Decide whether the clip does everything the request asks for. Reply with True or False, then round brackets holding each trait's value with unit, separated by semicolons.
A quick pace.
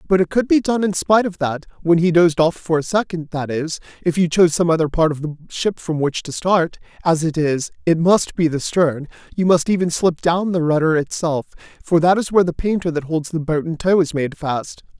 True (250 wpm)